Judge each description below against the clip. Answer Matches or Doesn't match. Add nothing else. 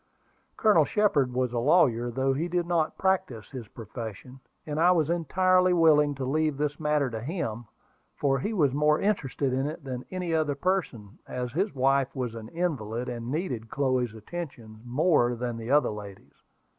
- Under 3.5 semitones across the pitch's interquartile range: Doesn't match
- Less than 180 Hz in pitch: Matches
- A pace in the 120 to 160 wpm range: Doesn't match